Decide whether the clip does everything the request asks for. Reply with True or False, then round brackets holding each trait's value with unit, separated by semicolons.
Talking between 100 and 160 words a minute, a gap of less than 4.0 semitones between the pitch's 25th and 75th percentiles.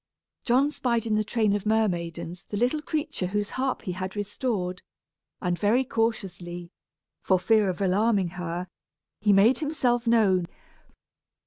False (140 wpm; 4.3 semitones)